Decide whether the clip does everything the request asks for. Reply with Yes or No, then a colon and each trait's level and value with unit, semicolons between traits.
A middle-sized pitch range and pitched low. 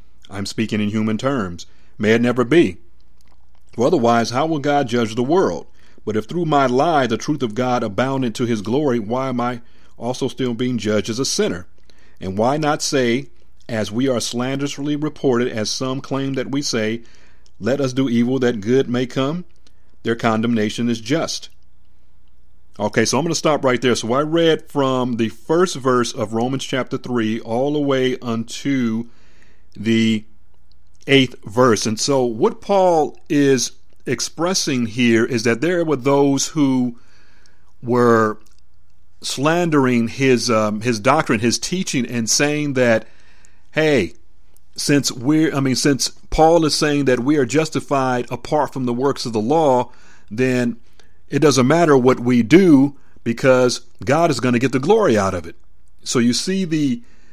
Yes: average, 3.9 semitones; low, 125 Hz